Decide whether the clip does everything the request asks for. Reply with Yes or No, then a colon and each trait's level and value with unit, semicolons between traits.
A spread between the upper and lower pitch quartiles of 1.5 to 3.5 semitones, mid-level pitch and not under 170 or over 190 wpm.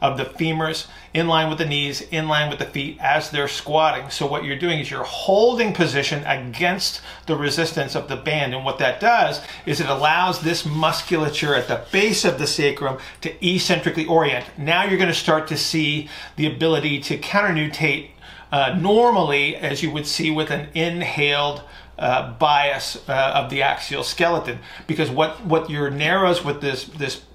Yes: narrow, 2.6 semitones; medium, 155 Hz; average, 185 wpm